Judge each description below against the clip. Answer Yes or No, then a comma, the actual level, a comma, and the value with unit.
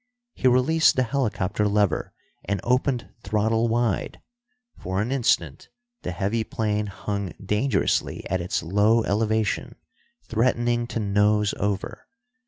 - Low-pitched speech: Yes, low, 105 Hz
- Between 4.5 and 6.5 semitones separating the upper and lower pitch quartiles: No, average, 2.9 semitones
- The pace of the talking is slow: Yes, slow, 120 wpm